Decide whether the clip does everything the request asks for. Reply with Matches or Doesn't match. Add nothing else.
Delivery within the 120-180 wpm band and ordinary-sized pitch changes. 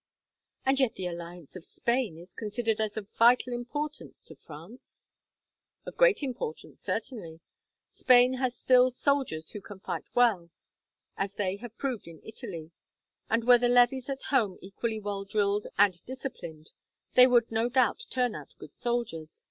Matches